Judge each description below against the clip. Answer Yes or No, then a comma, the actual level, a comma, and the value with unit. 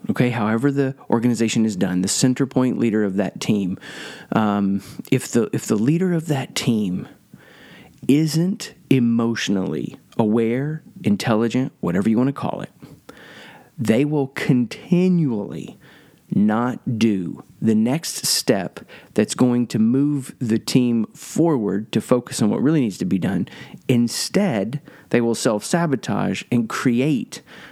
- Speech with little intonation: No, average, 3.7 semitones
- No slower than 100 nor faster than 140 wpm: Yes, slow, 135 wpm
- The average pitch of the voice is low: Yes, low, 120 Hz